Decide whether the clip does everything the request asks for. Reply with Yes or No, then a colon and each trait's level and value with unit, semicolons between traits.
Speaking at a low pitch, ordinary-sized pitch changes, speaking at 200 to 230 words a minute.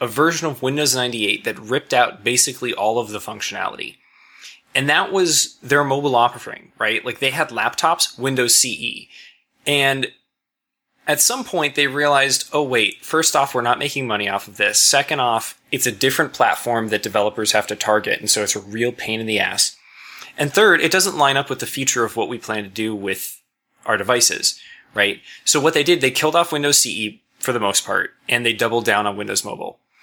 Yes: low, 130 Hz; average, 5.0 semitones; fast, 205 wpm